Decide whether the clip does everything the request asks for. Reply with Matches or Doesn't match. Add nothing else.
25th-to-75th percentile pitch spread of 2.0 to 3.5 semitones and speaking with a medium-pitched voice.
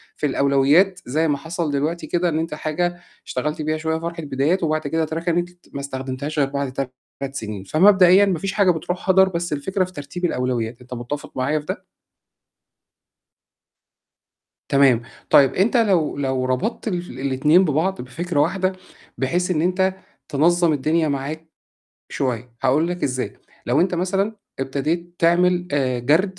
Doesn't match